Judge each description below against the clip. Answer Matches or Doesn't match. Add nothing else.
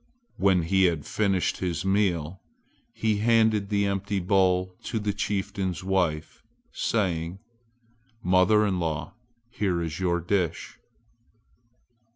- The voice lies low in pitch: Matches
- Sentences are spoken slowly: Matches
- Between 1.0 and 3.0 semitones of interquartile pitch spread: Matches